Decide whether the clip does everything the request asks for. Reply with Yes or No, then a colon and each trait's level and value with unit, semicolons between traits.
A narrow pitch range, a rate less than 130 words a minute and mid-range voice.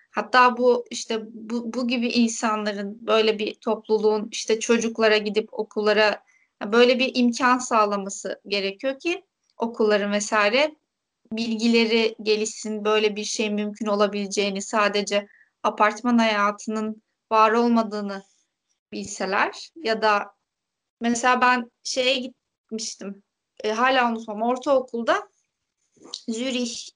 No: narrow, 2.3 semitones; average, 100 wpm; high, 220 Hz